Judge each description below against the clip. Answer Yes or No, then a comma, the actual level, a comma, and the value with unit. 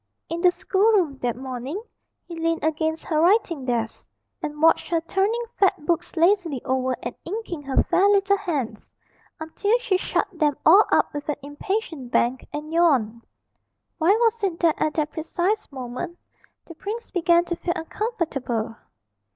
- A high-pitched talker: Yes, very high, 330 Hz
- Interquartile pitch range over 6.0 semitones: No, average, 5.2 semitones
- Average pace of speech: Yes, average, 160 wpm